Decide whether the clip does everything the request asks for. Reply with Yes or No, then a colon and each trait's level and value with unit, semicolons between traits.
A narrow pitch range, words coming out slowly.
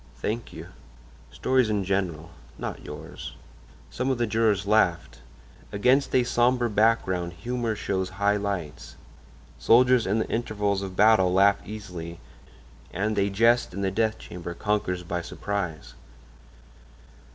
No: average, 3.9 semitones; slow, 130 wpm